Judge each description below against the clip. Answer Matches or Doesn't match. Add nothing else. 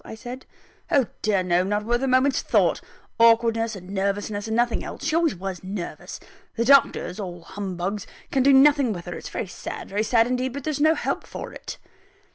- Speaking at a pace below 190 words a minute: Doesn't match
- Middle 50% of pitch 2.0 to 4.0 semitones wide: Doesn't match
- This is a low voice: Doesn't match